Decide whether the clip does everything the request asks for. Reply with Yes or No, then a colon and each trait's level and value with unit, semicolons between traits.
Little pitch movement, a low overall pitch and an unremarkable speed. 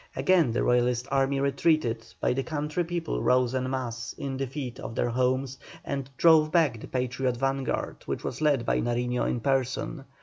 Yes: narrow, 2.3 semitones; low, 130 Hz; average, 175 wpm